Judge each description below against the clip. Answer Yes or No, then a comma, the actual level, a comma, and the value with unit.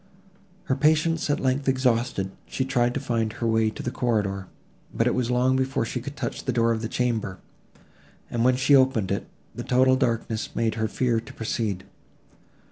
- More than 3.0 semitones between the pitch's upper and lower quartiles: No, narrow, 2.6 semitones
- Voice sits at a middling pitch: No, low, 125 Hz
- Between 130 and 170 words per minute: No, average, 200 wpm